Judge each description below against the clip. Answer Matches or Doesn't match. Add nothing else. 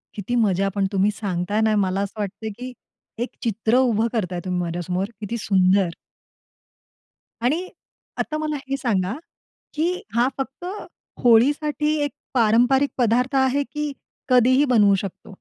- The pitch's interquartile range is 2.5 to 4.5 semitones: Doesn't match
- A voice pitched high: Matches